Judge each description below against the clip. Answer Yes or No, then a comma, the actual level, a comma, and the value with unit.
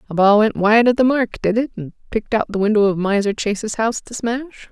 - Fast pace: Yes, fast, 255 wpm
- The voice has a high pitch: Yes, high, 220 Hz